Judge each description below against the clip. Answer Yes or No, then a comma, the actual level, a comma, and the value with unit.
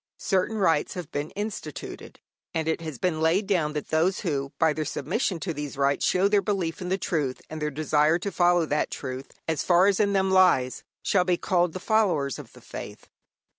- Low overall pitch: No, medium, 165 Hz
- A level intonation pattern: No, average, 3.9 semitones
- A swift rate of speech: Yes, fast, 210 wpm